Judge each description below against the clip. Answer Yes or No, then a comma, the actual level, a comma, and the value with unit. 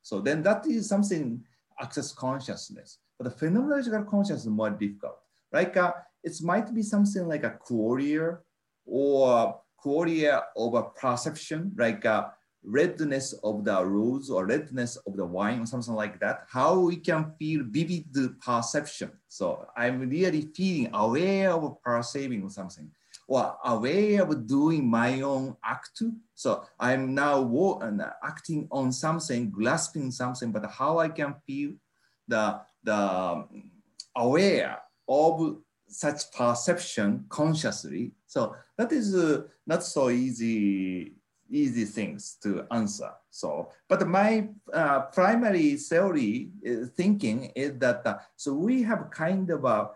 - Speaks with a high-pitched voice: No, medium, 145 Hz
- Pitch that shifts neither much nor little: No, wide, 6.7 semitones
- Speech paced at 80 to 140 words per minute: Yes, slow, 135 wpm